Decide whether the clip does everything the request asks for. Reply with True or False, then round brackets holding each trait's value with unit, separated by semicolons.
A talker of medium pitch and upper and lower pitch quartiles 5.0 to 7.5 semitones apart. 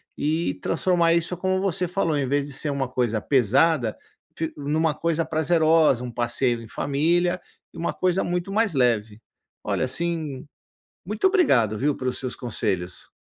True (150 Hz; 5.3 semitones)